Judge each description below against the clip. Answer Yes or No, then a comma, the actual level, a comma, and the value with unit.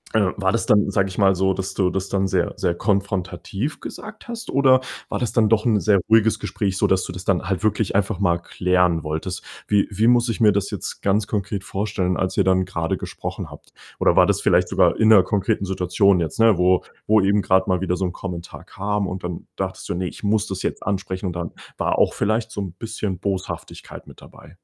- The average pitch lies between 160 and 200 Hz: No, very low, 95 Hz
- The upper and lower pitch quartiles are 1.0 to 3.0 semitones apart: Yes, narrow, 2.4 semitones